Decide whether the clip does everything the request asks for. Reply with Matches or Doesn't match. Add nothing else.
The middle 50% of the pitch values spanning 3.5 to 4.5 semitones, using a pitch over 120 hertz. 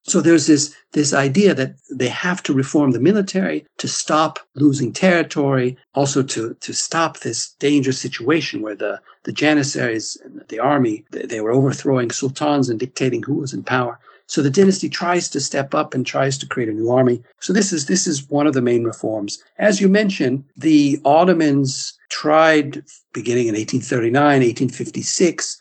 Matches